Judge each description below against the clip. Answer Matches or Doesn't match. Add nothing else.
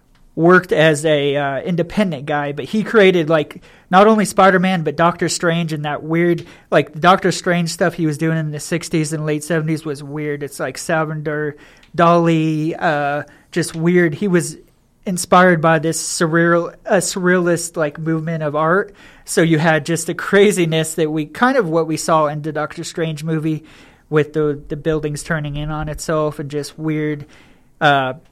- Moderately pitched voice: Matches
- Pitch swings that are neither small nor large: Doesn't match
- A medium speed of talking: Matches